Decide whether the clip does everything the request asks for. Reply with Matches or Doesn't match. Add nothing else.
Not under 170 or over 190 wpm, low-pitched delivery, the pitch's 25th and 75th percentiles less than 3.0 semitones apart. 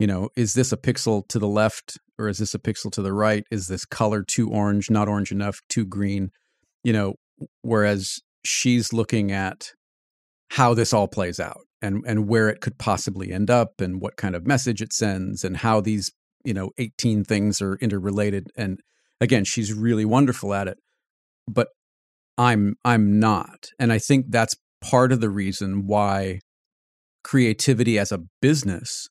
Matches